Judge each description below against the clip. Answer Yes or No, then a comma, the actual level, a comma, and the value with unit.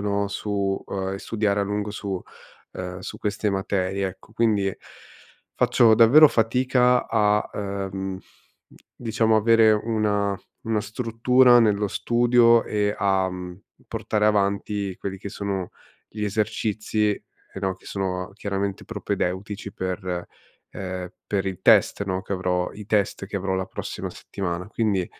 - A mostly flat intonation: Yes, narrow, 2.1 semitones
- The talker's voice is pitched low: Yes, low, 100 Hz